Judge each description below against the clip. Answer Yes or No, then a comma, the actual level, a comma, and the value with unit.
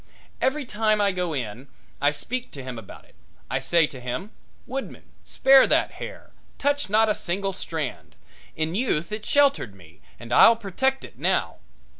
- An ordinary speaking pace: Yes, average, 170 wpm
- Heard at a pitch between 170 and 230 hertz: Yes, high, 190 Hz